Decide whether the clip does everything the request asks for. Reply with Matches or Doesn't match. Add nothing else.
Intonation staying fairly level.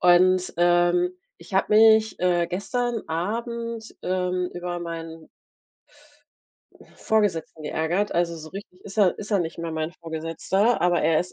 Doesn't match